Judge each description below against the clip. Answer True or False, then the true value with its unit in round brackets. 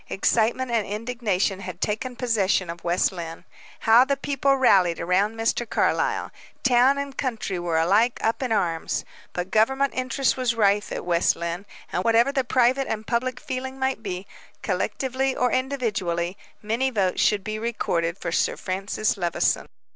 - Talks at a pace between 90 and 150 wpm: False (160 wpm)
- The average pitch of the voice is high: True (220 Hz)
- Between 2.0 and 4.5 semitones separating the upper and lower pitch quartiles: False (5.5 semitones)